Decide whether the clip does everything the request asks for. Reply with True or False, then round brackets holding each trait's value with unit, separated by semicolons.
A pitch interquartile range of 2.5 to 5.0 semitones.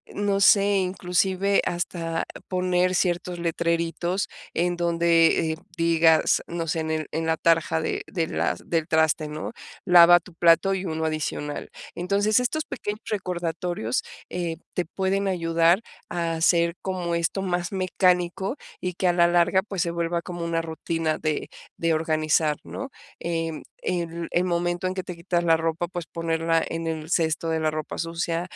False (1.7 semitones)